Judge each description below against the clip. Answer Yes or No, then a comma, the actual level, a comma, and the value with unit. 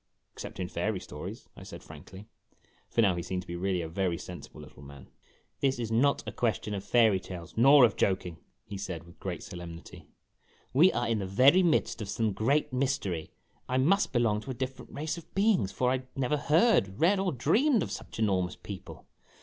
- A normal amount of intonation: No, wide, 6.7 semitones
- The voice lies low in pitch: Yes, low, 115 Hz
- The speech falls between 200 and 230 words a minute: Yes, fast, 205 wpm